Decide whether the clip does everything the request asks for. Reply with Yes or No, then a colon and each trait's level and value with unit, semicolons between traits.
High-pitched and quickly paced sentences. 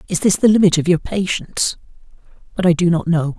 No: medium, 175 Hz; fast, 215 wpm